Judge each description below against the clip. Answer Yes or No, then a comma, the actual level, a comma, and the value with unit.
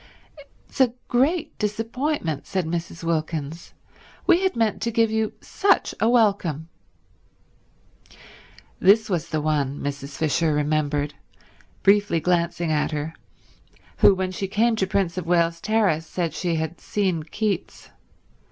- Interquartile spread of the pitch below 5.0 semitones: No, wide, 5.5 semitones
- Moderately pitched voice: Yes, medium, 175 Hz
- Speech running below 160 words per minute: Yes, slow, 135 wpm